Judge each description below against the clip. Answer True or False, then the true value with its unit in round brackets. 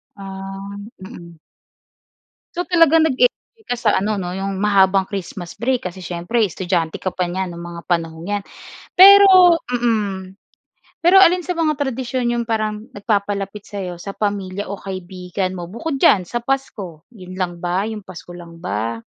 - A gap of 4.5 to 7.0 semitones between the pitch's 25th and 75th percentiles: True (4.8 semitones)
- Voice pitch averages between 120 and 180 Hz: False (195 Hz)